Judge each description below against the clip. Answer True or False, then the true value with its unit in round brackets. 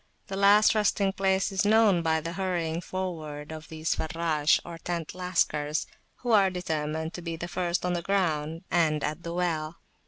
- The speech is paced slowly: False (180 wpm)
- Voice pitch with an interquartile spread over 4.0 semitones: False (3.0 semitones)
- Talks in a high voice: False (170 Hz)